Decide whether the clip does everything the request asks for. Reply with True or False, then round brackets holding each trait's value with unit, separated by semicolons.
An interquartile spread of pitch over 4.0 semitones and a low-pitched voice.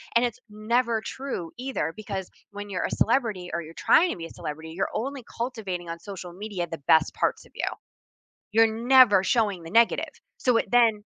False (4.9 semitones; 210 Hz)